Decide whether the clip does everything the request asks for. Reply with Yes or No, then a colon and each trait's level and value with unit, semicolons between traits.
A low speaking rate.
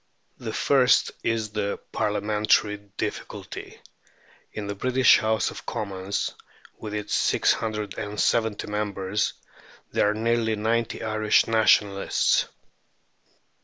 Yes: slow, 110 wpm